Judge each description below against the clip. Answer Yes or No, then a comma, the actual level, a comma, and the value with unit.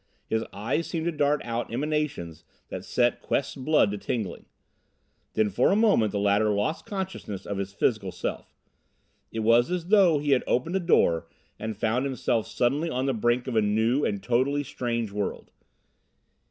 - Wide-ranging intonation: Yes, wide, 5.8 semitones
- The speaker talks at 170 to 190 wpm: Yes, average, 175 wpm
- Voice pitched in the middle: No, low, 120 Hz